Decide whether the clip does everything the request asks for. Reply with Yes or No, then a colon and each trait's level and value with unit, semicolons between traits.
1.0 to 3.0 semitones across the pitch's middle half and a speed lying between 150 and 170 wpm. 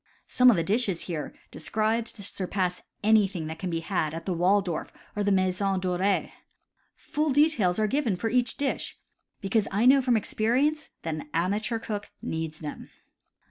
No: average, 4.3 semitones; average, 165 wpm